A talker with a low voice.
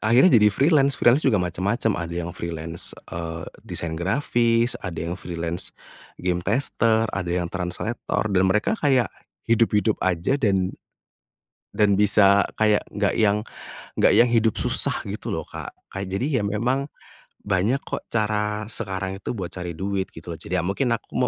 Yes: low, 100 Hz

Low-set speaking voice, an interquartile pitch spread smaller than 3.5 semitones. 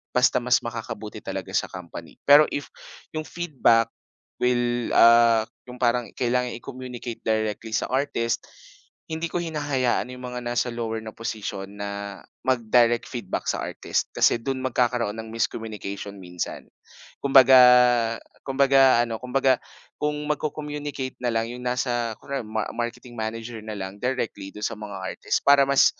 Yes: low, 120 Hz; average, 2.8 semitones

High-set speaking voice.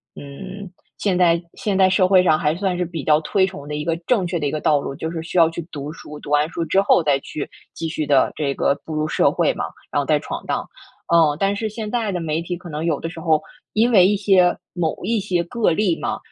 No: medium, 170 Hz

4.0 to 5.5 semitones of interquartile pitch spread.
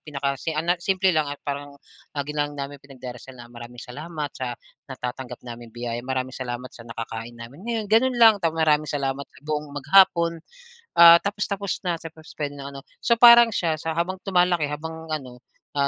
Yes: average, 4.6 semitones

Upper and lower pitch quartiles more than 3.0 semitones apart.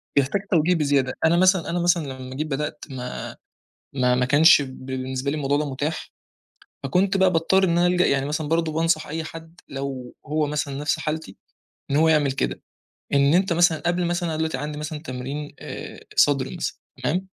Yes: average, 3.4 semitones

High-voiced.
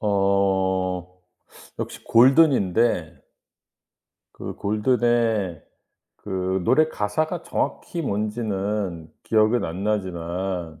No: low, 100 Hz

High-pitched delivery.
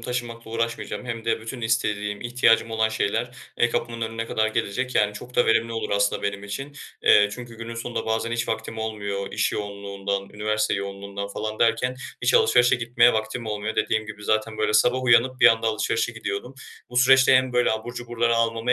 No: low, 115 Hz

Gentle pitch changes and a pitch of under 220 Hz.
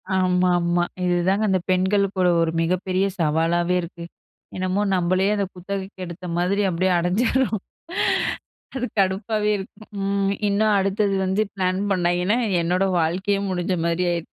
Yes: narrow, 2.0 semitones; medium, 185 Hz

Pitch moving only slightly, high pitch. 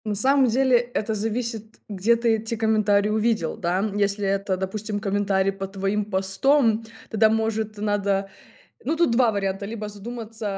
Yes: narrow, 2.3 semitones; high, 215 Hz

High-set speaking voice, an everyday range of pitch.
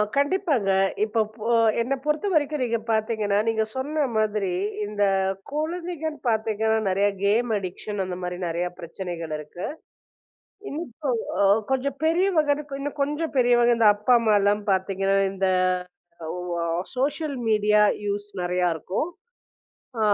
No: high, 220 Hz; wide, 6.5 semitones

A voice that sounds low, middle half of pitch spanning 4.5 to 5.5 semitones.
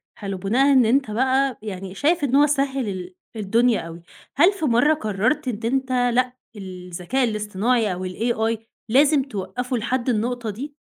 No: high, 240 Hz; average, 4.8 semitones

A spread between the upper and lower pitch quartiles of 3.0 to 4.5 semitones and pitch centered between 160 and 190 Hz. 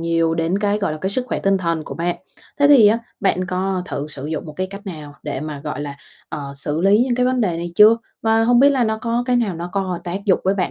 No: average, 5.0 semitones; medium, 185 Hz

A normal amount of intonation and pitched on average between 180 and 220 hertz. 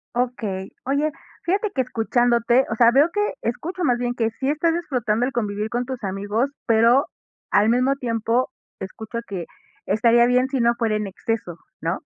No: average, 3.1 semitones; high, 240 Hz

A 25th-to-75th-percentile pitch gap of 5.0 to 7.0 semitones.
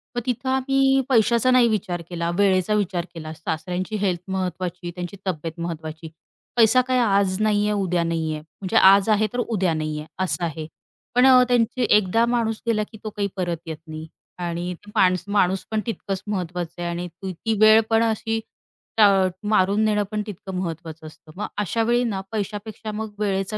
No: average, 4.1 semitones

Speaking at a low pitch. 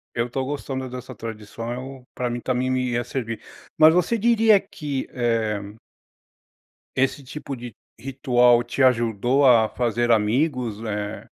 Yes: low, 125 Hz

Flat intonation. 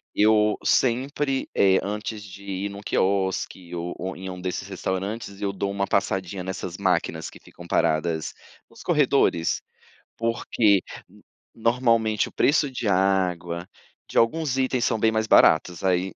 No: average, 3.3 semitones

